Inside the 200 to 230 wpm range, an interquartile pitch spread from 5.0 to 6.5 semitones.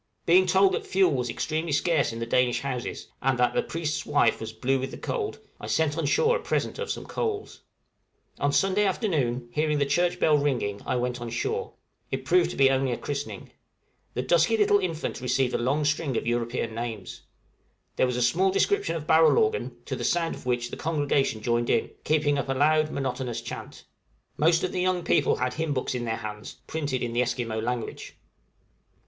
Yes: fast, 205 wpm; average, 5.3 semitones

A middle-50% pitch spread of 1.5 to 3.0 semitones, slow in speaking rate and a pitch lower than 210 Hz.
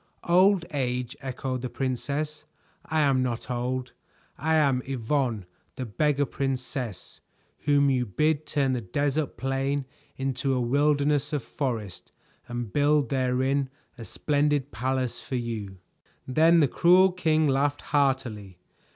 Yes: average, 2.7 semitones; slow, 130 wpm; low, 135 Hz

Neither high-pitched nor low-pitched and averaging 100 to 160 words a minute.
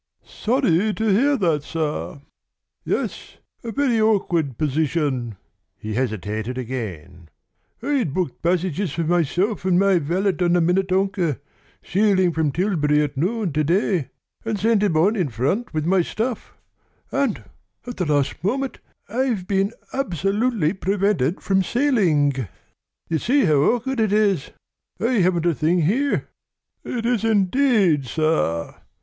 Yes: medium, 180 Hz; average, 140 wpm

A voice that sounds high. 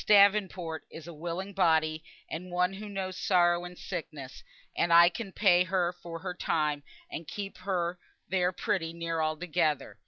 No: medium, 175 Hz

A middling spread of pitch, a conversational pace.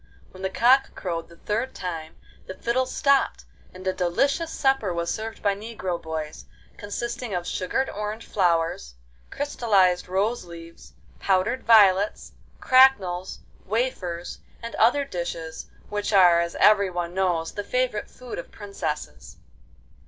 No: average, 5.0 semitones; slow, 130 wpm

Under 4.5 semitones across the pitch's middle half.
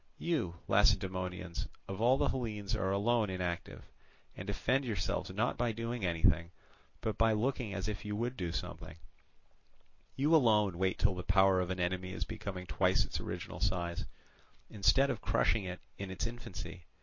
Yes: average, 4.0 semitones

